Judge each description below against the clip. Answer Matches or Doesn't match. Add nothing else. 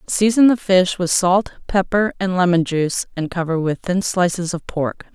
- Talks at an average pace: Matches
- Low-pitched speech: Doesn't match